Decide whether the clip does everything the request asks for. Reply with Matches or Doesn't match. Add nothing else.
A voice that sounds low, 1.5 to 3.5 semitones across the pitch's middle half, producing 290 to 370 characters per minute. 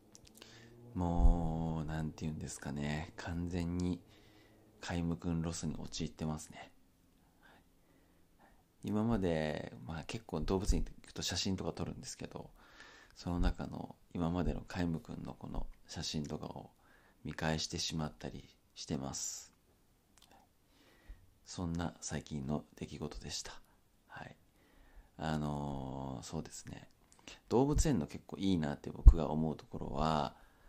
Doesn't match